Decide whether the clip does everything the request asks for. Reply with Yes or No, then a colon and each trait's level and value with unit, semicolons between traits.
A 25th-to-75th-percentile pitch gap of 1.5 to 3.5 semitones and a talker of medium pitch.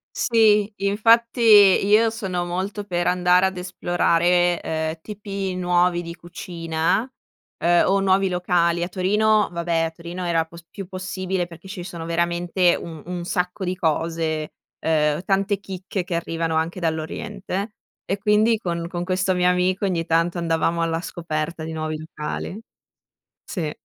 Yes: narrow, 2.5 semitones; medium, 180 Hz